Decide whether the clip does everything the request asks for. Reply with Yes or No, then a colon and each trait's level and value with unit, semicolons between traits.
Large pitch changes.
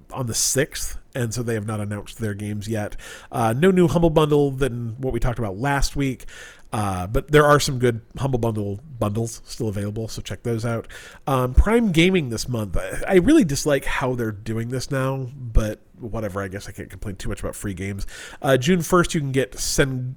No: average, 4.6 semitones